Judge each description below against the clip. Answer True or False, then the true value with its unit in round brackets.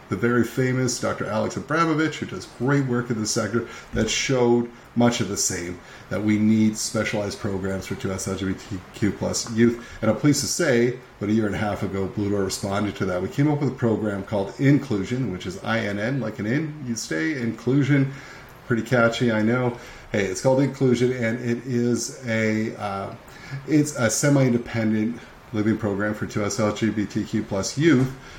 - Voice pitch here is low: True (115 Hz)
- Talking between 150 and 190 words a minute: False (205 wpm)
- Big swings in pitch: False (3.4 semitones)